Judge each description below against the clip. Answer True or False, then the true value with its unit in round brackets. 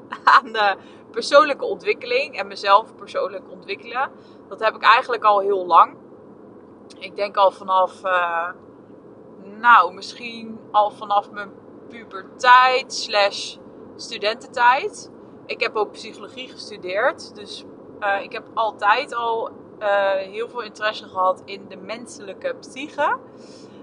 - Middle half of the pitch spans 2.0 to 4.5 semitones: True (3.7 semitones)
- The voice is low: False (215 Hz)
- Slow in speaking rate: True (115 wpm)